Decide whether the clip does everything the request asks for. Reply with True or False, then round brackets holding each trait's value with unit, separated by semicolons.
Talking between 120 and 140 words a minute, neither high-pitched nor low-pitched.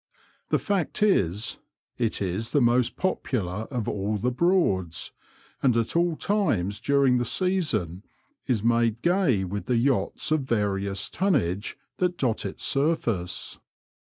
False (135 wpm; 120 Hz)